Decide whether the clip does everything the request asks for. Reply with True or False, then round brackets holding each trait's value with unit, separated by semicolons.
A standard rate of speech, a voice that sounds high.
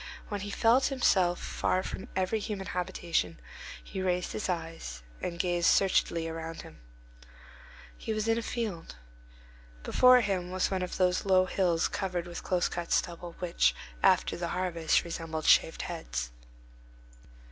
False (145 wpm; 180 Hz)